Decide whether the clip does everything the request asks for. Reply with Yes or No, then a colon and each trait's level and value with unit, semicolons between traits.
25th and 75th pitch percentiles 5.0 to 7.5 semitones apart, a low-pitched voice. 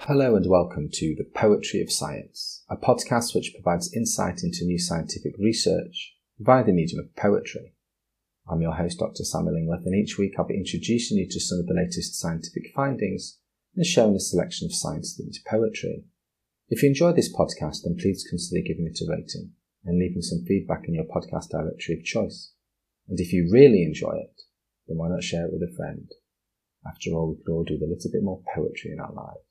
Yes: average, 5.3 semitones; very low, 90 Hz